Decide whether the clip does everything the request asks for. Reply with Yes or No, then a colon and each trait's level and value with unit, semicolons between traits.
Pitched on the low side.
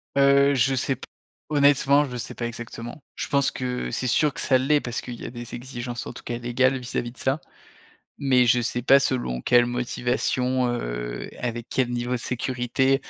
Yes: low, 125 Hz